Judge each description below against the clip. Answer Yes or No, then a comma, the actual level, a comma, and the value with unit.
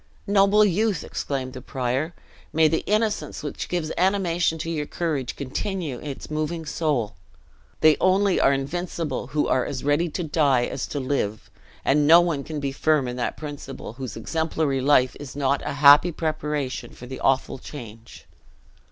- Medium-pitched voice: Yes, medium, 150 Hz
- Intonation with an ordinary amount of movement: Yes, average, 3.7 semitones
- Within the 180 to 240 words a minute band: No, average, 165 wpm